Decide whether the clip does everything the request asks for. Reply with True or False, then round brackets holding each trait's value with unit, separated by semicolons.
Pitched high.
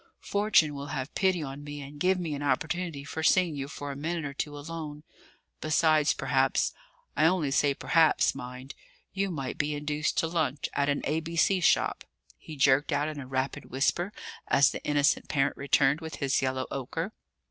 False (145 Hz)